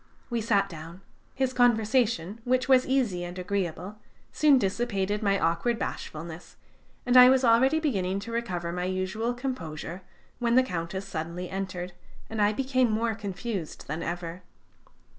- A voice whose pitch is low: No, high, 205 Hz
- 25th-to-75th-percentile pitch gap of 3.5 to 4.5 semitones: No, average, 5.3 semitones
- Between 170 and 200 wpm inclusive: No, average, 145 wpm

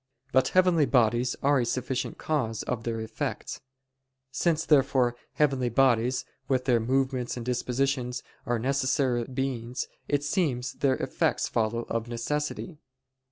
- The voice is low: Yes, low, 130 Hz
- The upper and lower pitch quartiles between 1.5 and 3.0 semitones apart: Yes, narrow, 2.4 semitones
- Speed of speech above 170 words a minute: No, slow, 135 wpm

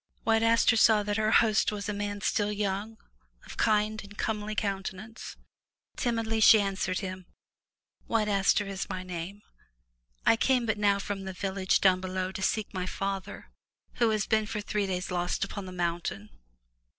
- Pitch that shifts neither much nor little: No, narrow, 2.3 semitones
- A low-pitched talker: No, high, 205 Hz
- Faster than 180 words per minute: No, average, 175 wpm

